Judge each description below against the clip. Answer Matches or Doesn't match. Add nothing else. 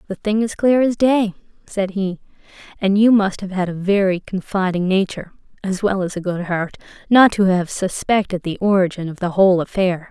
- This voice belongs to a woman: Matches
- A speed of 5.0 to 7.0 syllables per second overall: Matches